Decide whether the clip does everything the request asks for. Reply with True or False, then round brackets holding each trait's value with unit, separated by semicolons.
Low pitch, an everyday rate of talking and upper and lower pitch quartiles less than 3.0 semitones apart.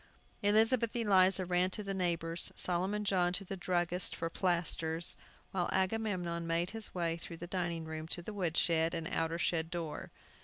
False (175 Hz; 170 wpm; 2.4 semitones)